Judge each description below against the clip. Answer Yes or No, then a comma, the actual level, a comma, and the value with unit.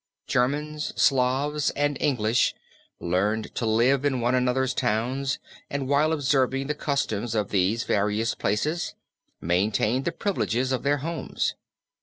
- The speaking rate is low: Yes, slow, 130 wpm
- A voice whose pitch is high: No, low, 130 Hz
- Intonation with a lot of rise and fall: No, average, 4.4 semitones